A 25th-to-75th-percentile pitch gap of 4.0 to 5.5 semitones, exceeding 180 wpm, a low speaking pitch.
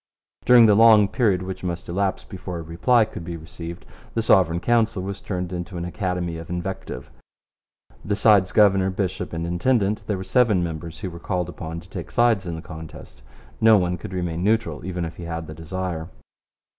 No: average, 3.2 semitones; average, 190 wpm; very low, 90 Hz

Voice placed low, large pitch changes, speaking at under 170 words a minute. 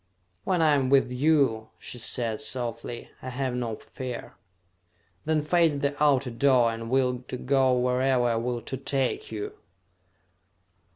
No: low, 130 Hz; narrow, 2.6 semitones; average, 150 wpm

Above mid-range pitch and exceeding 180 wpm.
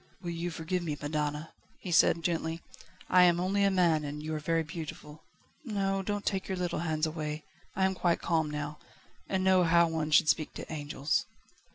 No: medium, 165 Hz; average, 195 wpm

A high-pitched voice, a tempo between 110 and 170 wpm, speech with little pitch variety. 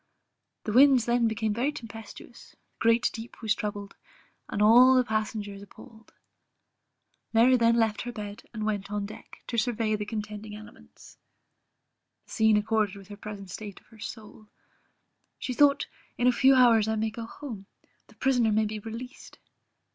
Yes: high, 220 Hz; average, 165 wpm; narrow, 2.2 semitones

